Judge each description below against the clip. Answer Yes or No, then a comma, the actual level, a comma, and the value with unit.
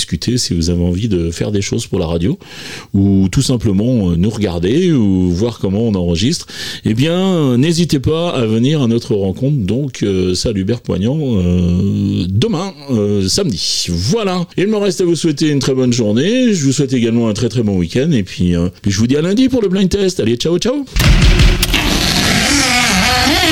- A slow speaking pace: No, average, 185 wpm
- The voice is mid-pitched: No, low, 120 Hz